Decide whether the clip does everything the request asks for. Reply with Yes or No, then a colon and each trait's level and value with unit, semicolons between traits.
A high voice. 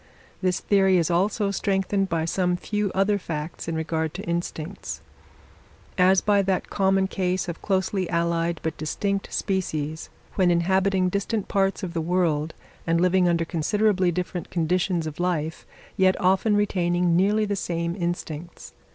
No: medium, 180 Hz